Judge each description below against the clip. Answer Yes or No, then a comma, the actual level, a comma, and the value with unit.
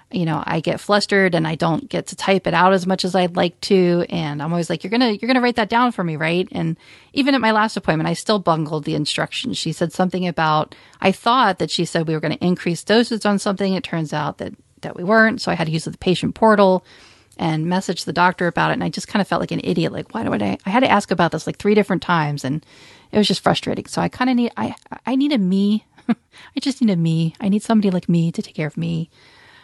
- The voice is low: No, medium, 185 Hz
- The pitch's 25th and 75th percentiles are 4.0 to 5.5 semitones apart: Yes, average, 4.4 semitones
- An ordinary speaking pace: No, fast, 275 wpm